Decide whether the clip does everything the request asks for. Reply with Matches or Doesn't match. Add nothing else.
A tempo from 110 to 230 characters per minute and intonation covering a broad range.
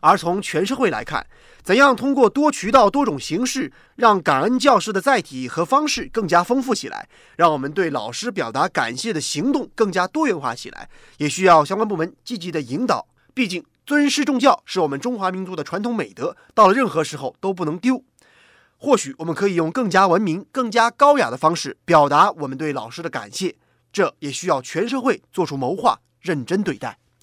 Doesn't match